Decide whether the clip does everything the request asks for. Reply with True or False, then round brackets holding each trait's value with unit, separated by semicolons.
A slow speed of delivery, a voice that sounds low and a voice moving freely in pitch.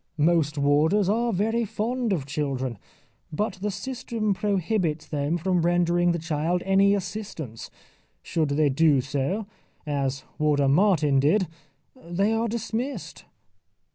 False (125 wpm; 175 Hz; 6.0 semitones)